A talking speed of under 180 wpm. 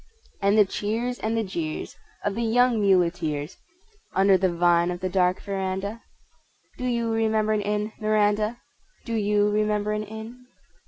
Yes: average, 155 wpm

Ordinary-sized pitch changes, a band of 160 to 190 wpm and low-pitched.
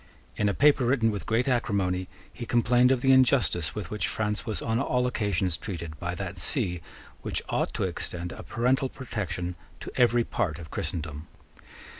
No: wide, 5.8 semitones; average, 175 wpm; low, 105 Hz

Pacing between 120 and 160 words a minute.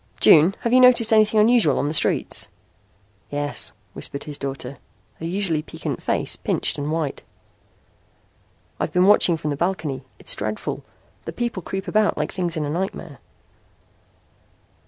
Yes: average, 150 wpm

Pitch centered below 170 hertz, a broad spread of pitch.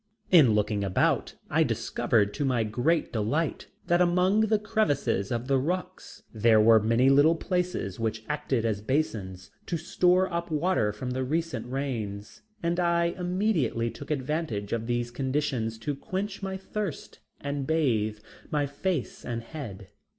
Yes: low, 135 Hz; wide, 7.2 semitones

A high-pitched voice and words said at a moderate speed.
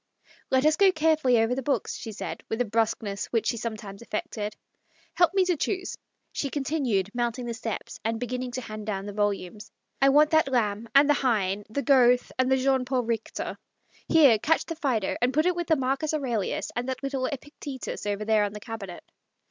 No: high, 245 Hz; fast, 210 wpm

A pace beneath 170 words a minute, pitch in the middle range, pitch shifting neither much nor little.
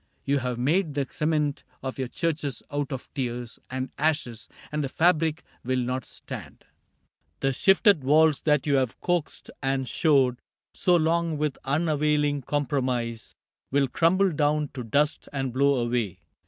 Yes: average, 150 wpm; medium, 145 Hz; average, 3.1 semitones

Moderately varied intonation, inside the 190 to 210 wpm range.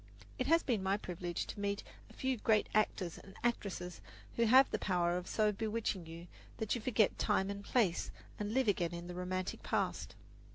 Yes: average, 3.7 semitones; average, 195 wpm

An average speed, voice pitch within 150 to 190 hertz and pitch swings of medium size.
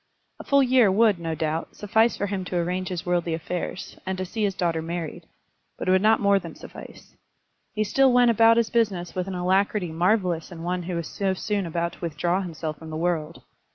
No: fast, 220 wpm; medium, 185 Hz; average, 3.4 semitones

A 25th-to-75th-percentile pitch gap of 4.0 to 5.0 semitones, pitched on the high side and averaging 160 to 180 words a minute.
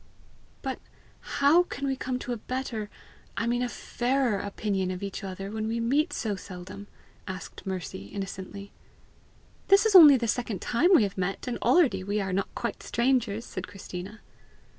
Yes: average, 4.6 semitones; high, 215 Hz; average, 170 wpm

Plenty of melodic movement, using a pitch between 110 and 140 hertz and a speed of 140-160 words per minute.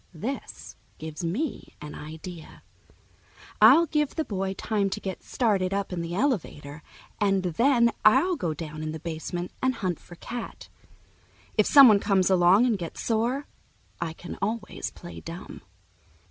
No: wide, 5.7 semitones; high, 195 Hz; average, 150 wpm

